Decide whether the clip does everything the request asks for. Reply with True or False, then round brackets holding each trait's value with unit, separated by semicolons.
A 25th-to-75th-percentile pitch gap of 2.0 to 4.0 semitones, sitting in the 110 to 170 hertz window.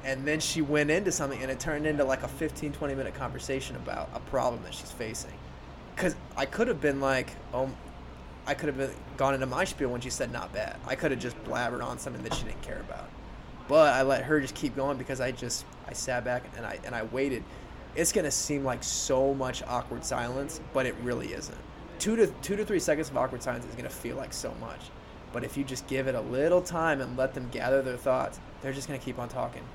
True (2.7 semitones; 135 Hz)